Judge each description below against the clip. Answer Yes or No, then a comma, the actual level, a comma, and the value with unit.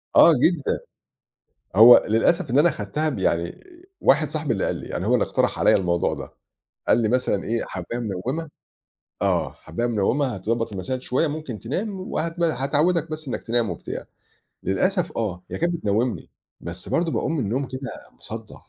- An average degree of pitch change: No, wide, 6.6 semitones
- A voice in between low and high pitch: No, low, 125 Hz